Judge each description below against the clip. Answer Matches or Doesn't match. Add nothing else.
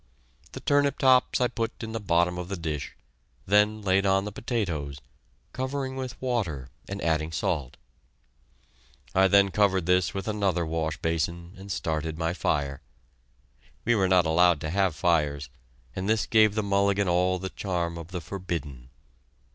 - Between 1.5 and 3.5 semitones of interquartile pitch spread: Doesn't match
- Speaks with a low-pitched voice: Matches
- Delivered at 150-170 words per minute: Matches